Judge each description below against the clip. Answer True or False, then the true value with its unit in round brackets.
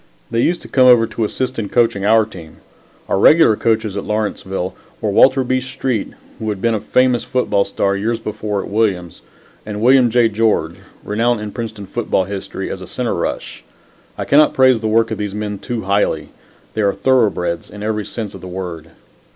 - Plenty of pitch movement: False (2.9 semitones)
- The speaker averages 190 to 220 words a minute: True (195 wpm)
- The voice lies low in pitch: True (110 Hz)